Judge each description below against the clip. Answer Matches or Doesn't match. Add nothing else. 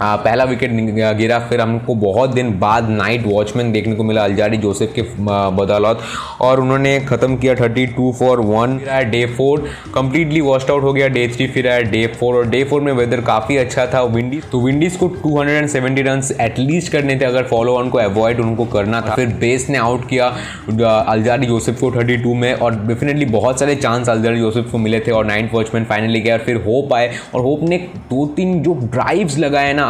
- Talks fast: Matches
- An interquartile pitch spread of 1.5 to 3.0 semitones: Matches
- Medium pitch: Doesn't match